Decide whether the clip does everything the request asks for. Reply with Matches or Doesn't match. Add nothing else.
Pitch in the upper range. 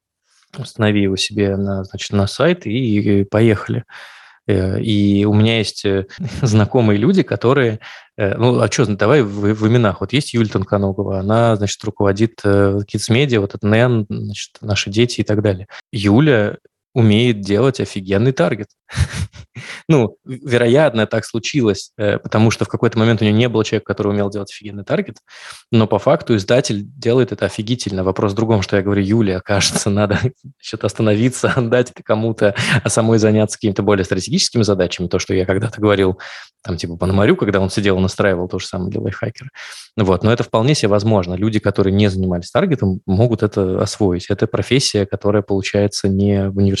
Doesn't match